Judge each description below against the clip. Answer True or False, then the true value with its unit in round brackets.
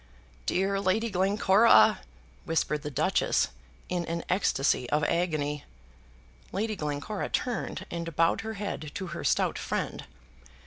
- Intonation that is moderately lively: True (4.7 semitones)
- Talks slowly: True (125 wpm)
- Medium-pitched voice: True (175 Hz)